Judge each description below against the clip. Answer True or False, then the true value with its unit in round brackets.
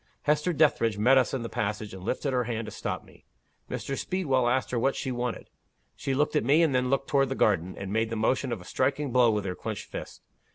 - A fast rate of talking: True (245 wpm)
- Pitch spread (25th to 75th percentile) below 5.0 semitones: True (3.7 semitones)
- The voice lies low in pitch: True (125 Hz)